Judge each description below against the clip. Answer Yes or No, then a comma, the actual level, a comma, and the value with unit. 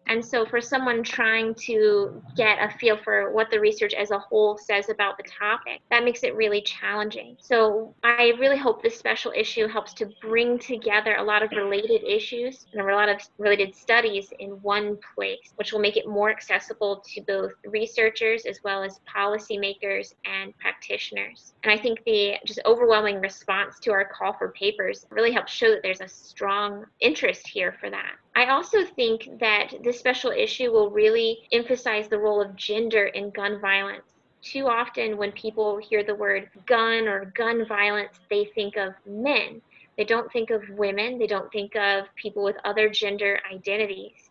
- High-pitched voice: Yes, high, 215 Hz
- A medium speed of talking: Yes, average, 180 wpm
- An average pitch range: Yes, average, 3.0 semitones